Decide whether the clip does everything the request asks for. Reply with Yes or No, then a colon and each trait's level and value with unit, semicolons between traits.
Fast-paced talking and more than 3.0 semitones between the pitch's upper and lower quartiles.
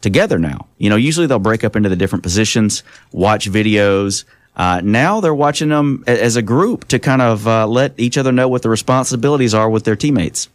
Yes: fast, 210 wpm; average, 3.6 semitones